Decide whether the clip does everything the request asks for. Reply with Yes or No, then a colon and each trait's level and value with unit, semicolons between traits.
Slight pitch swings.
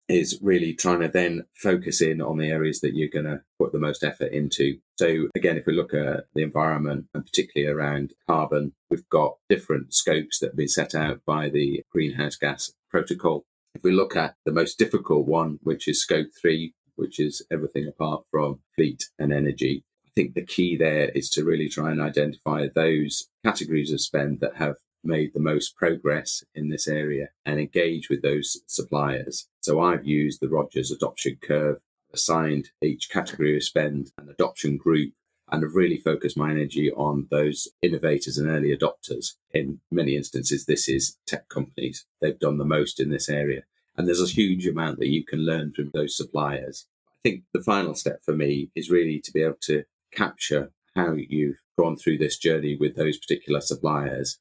Yes: narrow, 1.4 semitones